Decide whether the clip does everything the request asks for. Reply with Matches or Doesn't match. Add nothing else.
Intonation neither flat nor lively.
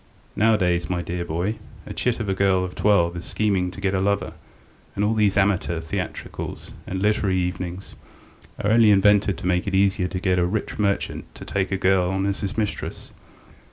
Doesn't match